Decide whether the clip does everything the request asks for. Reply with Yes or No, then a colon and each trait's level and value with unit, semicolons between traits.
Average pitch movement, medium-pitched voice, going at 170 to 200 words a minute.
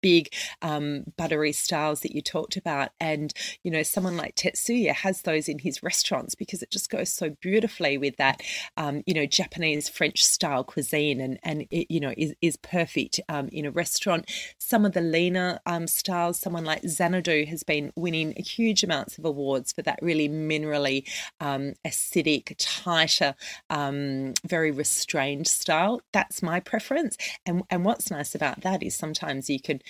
Yes: average, 3.3 semitones; medium, 160 Hz; average, 175 wpm